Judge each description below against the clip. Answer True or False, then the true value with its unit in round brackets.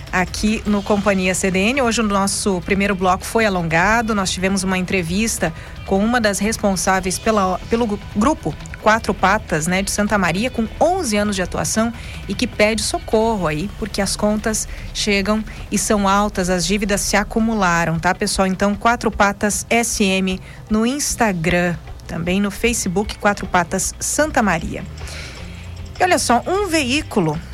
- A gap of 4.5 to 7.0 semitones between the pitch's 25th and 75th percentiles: False (3.0 semitones)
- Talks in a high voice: True (205 Hz)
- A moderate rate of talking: True (150 wpm)